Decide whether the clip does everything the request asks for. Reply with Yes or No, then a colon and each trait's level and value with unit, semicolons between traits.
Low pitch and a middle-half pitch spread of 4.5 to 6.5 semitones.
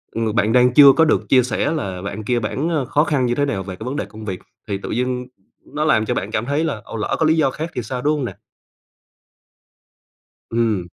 Yes: low, 125 Hz; average, 5.1 semitones